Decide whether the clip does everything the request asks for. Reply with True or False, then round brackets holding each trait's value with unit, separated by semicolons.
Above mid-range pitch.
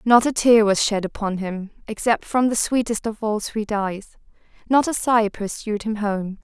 True (215 Hz)